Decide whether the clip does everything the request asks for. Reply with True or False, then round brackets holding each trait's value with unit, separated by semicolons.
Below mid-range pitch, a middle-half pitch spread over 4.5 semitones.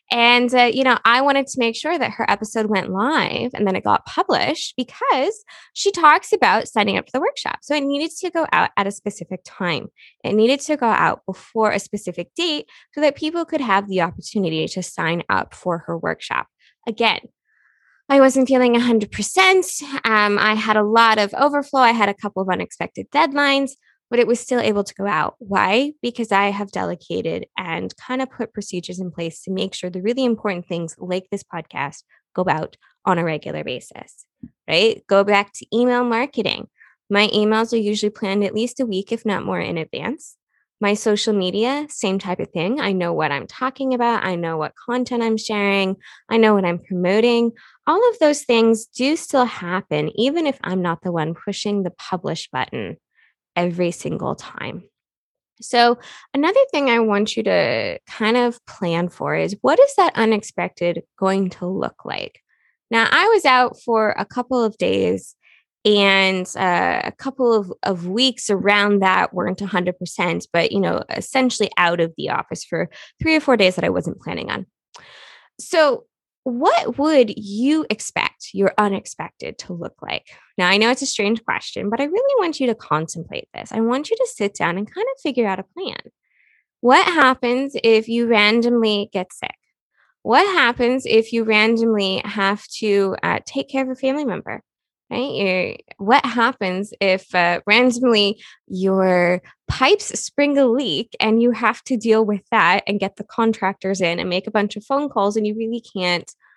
False (225 Hz; 5.1 semitones)